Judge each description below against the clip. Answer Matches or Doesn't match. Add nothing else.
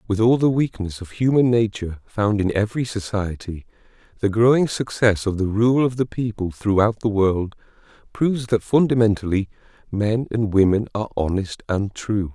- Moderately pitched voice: Doesn't match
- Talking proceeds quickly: Doesn't match